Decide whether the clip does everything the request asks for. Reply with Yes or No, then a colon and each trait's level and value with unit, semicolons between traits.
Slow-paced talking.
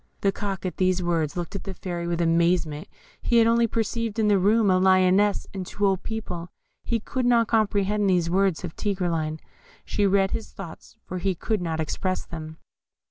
No: average, 190 wpm